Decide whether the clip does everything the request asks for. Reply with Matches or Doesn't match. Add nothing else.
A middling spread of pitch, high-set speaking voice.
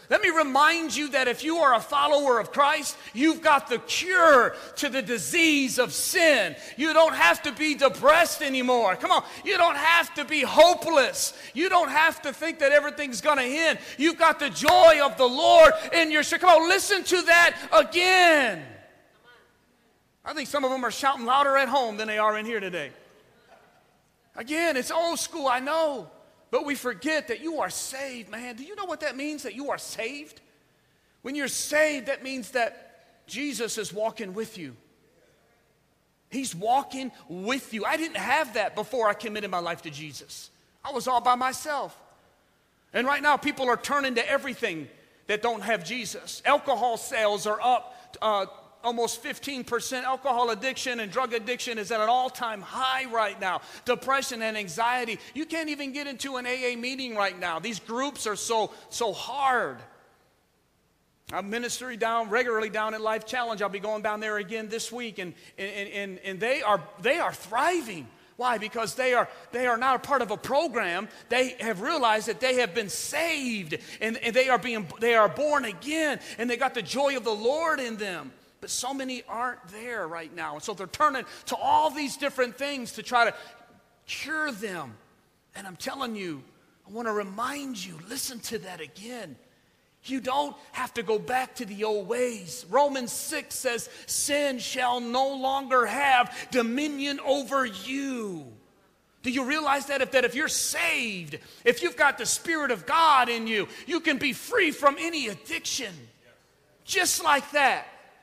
Matches